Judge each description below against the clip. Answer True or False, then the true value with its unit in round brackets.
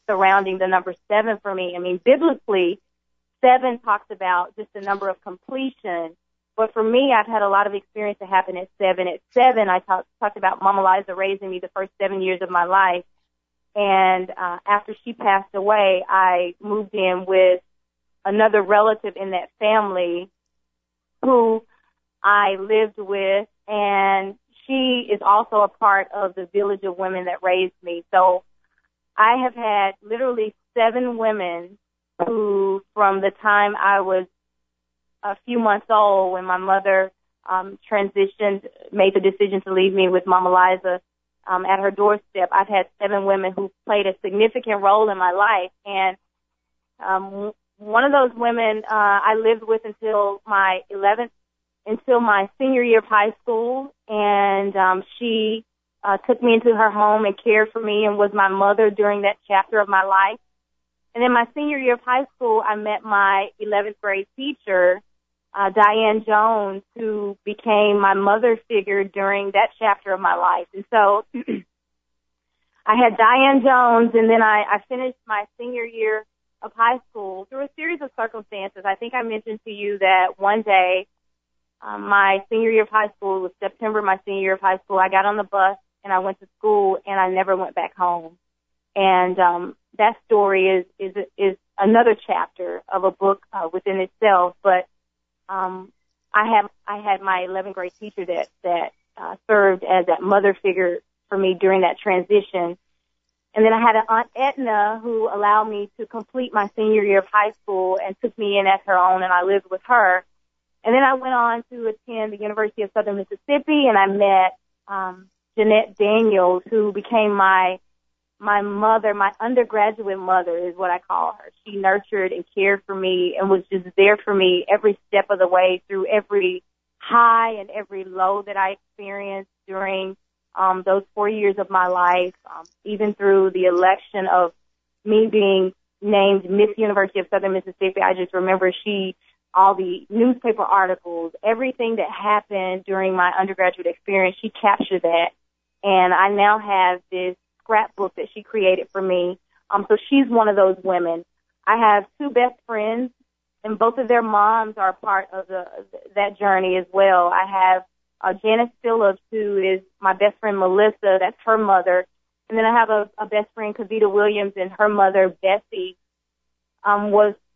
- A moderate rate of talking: True (175 wpm)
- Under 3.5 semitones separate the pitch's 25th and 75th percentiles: True (2.4 semitones)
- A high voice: True (200 Hz)